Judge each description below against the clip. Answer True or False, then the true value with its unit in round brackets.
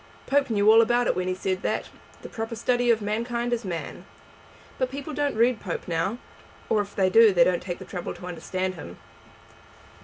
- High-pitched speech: True (215 Hz)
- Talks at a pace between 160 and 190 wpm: False (205 wpm)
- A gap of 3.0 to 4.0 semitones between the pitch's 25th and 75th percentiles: False (4.5 semitones)